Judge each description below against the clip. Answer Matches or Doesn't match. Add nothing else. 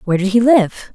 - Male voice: Doesn't match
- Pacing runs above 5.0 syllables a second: Matches